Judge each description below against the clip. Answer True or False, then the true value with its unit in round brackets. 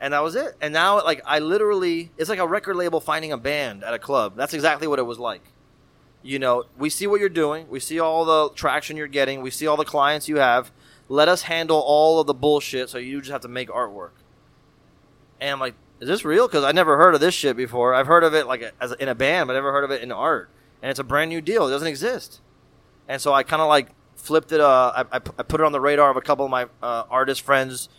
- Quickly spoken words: True (270 wpm)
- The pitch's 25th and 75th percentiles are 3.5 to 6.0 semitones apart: False (2.9 semitones)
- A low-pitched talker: False (145 Hz)